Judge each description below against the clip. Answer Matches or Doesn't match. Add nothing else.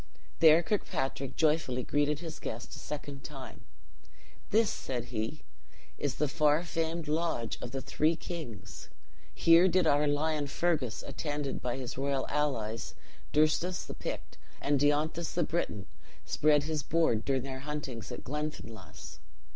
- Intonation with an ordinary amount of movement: Matches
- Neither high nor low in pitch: Matches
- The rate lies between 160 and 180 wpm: Doesn't match